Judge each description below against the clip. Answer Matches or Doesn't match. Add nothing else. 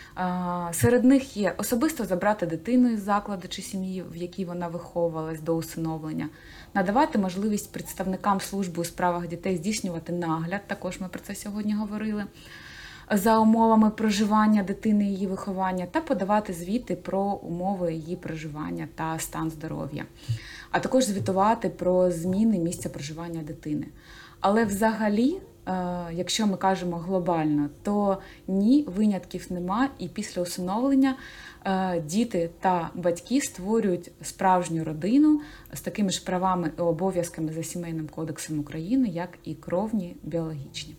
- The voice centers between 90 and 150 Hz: Doesn't match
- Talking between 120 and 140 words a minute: Matches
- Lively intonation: Doesn't match